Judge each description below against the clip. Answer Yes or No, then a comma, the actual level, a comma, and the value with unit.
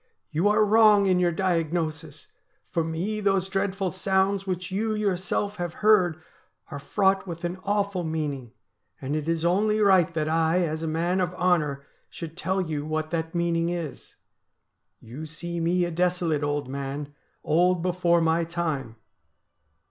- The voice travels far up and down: No, average, 3.1 semitones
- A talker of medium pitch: Yes, medium, 175 Hz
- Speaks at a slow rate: No, average, 160 wpm